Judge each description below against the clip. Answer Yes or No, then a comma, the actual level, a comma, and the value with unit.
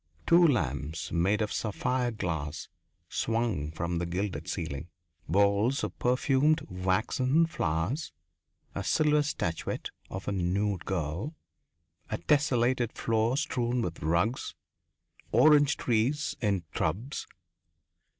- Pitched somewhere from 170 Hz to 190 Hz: No, low, 110 Hz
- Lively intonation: Yes, wide, 7.1 semitones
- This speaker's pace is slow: Yes, slow, 110 wpm